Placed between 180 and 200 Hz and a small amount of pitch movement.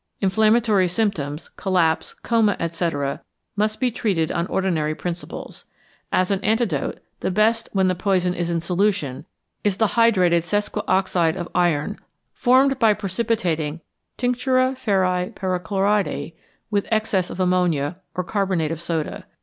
No: medium, 185 Hz; average, 3.9 semitones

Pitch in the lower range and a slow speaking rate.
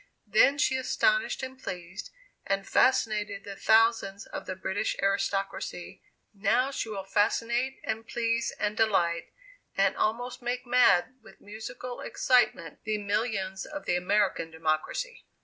No: high, 215 Hz; slow, 130 wpm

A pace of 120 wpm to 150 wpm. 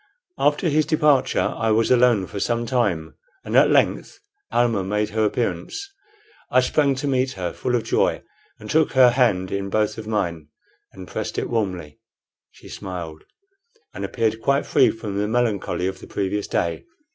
No: average, 170 wpm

